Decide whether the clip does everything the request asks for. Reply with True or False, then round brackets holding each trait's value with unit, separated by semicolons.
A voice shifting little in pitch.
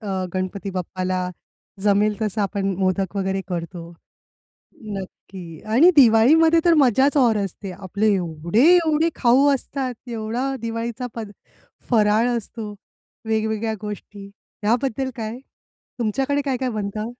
False (4.2 semitones)